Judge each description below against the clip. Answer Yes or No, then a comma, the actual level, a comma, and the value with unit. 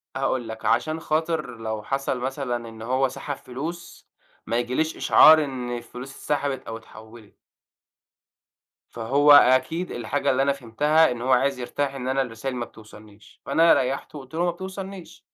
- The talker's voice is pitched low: Yes, low, 130 Hz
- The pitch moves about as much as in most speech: Yes, average, 3.7 semitones